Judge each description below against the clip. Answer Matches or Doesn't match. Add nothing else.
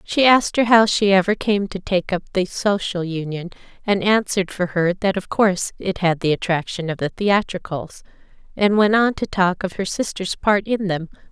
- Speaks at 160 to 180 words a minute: Doesn't match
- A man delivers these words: Doesn't match